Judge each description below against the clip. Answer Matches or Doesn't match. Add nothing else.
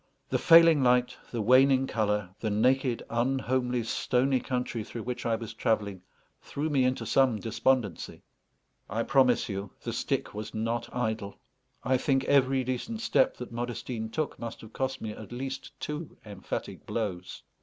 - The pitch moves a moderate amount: Matches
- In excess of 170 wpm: Doesn't match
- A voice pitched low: Matches